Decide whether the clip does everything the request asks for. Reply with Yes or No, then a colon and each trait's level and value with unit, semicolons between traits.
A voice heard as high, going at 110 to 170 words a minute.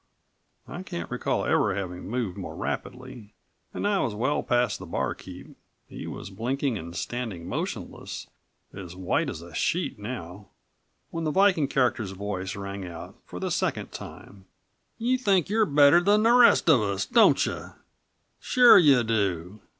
No: low, 115 Hz; average, 160 wpm